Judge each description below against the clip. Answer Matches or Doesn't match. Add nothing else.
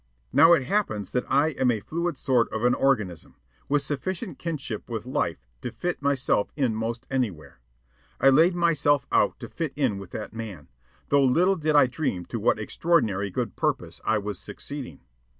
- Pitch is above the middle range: Doesn't match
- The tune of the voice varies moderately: Doesn't match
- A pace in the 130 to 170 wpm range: Doesn't match